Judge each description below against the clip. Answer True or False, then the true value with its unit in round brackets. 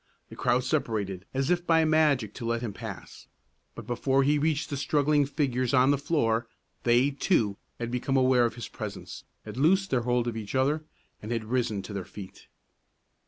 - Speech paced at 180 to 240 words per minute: True (190 wpm)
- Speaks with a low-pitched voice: True (130 Hz)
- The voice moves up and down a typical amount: True (3.8 semitones)